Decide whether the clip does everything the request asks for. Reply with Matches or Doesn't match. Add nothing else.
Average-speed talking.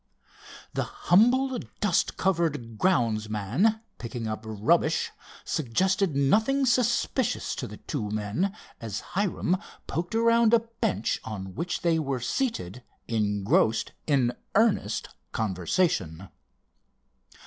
Doesn't match